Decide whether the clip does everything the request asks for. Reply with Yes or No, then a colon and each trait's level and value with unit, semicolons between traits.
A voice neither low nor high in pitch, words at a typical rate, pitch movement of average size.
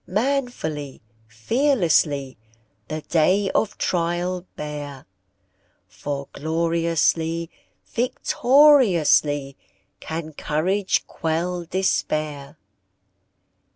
No: medium, 165 Hz; slow, 60 wpm; average, 4.2 semitones